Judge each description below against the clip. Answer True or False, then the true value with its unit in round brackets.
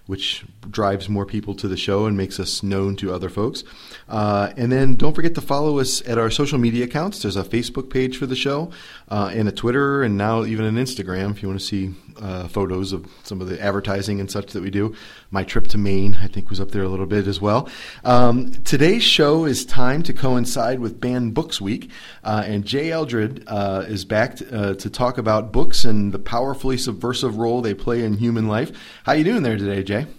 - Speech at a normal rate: False (225 wpm)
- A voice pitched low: True (110 Hz)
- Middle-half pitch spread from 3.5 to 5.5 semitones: True (4.1 semitones)